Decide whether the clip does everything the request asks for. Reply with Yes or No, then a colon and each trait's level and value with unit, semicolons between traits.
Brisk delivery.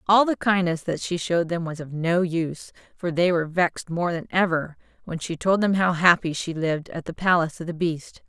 Yes: fast, 230 wpm